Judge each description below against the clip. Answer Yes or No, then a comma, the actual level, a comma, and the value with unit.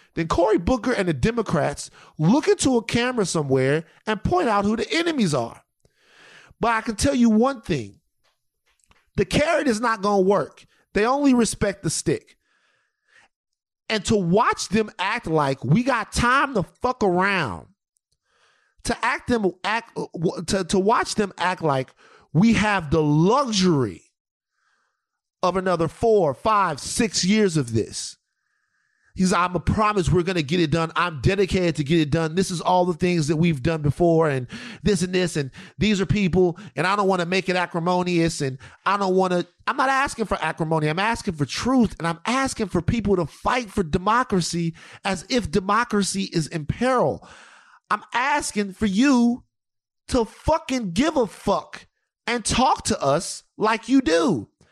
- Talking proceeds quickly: No, average, 170 wpm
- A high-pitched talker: Yes, high, 195 Hz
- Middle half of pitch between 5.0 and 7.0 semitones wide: Yes, wide, 5.4 semitones